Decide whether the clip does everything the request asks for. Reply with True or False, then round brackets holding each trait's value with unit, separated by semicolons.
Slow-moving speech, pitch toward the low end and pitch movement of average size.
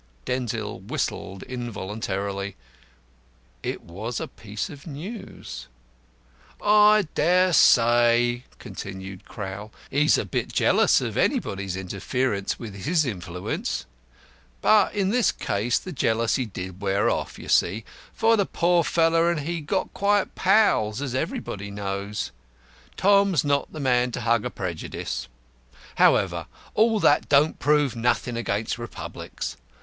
False (130 wpm; 120 Hz; 8.5 semitones)